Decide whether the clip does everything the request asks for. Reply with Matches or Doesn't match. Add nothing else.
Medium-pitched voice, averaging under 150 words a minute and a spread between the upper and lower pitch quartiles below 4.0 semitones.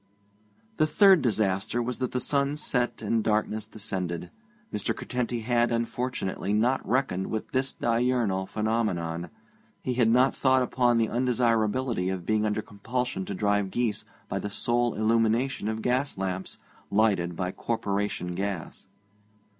Doesn't match